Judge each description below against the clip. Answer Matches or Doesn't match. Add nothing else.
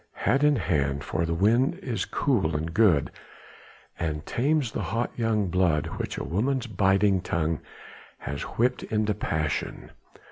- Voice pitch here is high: Doesn't match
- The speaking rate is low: Doesn't match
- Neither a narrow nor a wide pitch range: Doesn't match